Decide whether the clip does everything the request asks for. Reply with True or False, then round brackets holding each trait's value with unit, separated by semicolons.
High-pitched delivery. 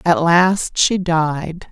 False (170 Hz)